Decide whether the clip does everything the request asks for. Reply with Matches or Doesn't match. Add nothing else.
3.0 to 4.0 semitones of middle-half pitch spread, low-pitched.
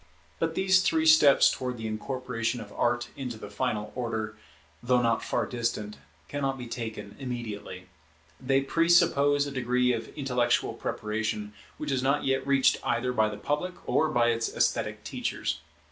Matches